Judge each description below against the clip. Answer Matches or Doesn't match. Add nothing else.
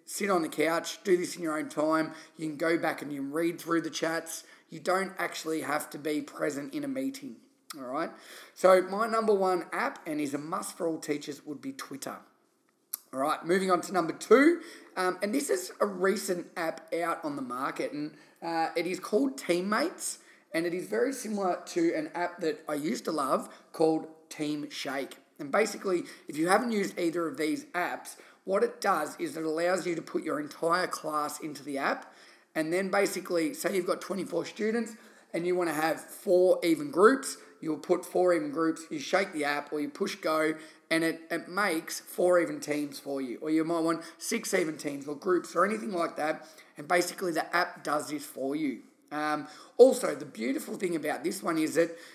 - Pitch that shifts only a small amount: Doesn't match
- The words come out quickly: Matches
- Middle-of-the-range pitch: Matches